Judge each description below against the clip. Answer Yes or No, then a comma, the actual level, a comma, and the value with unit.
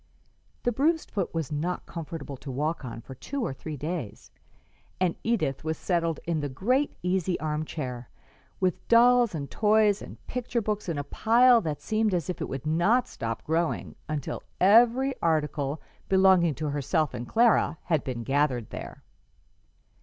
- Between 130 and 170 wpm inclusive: Yes, average, 165 wpm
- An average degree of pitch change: No, wide, 6.7 semitones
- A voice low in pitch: No, medium, 165 Hz